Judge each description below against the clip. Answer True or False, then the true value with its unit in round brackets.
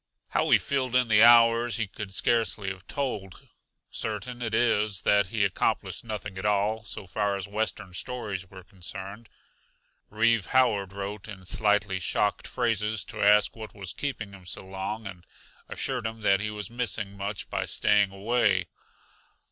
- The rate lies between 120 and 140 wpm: False (165 wpm)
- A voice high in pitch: False (105 Hz)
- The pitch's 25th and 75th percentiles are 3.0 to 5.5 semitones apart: False (2.6 semitones)